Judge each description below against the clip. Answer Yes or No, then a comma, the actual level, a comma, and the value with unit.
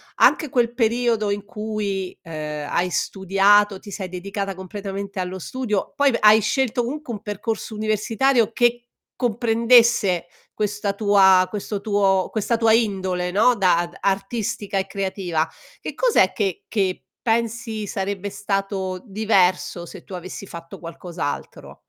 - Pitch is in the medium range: No, high, 200 Hz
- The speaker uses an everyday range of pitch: Yes, average, 3.0 semitones